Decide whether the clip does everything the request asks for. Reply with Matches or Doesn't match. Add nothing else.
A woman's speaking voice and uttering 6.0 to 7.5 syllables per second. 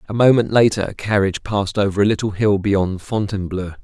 Doesn't match